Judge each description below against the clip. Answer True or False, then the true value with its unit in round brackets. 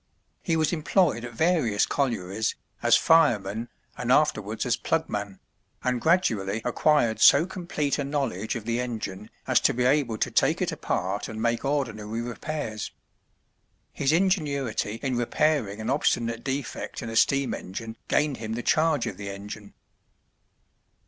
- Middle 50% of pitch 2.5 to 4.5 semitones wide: False (5.2 semitones)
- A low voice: True (120 Hz)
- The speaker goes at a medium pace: True (150 wpm)